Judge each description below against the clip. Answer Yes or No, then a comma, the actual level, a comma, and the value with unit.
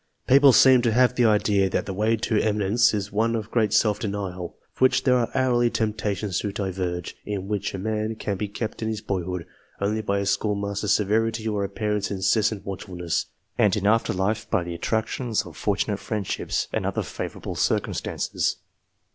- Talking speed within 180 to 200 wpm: Yes, average, 190 wpm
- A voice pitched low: Yes, low, 105 Hz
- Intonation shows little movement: Yes, narrow, 2.1 semitones